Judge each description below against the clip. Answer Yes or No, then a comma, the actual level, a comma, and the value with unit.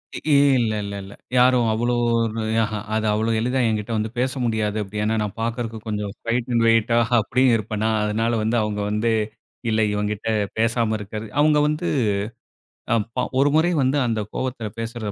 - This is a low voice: Yes, low, 110 Hz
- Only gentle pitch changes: Yes, narrow, 1.9 semitones